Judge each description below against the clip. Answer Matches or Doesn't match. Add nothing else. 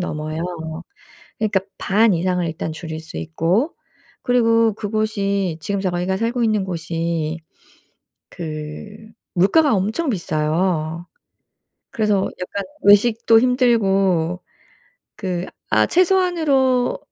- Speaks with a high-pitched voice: Matches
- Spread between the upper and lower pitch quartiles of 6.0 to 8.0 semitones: Doesn't match